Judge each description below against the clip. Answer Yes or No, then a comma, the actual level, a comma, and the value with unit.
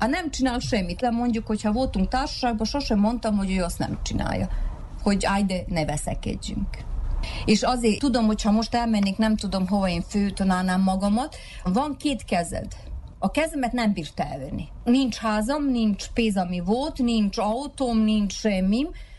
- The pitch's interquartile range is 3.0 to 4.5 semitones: Yes, average, 3.8 semitones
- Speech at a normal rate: No, fast, 160 wpm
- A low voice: No, high, 220 Hz